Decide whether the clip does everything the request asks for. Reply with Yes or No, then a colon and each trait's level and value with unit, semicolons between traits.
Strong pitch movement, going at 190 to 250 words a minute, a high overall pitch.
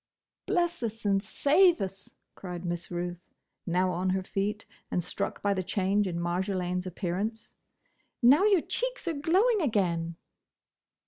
No: wide, 7.1 semitones; average, 140 wpm; high, 195 Hz